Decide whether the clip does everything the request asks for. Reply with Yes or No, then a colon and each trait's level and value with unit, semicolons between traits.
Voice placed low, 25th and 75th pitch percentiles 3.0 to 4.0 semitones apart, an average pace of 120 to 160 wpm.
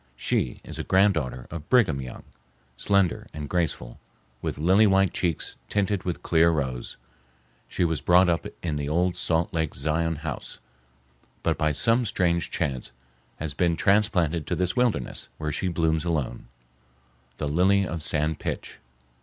Yes: very low, 85 Hz; average, 3.4 semitones; average, 155 wpm